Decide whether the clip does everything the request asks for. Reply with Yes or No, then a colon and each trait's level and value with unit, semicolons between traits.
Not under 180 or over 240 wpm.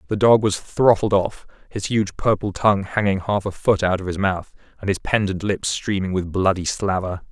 Yes: fast, 205 wpm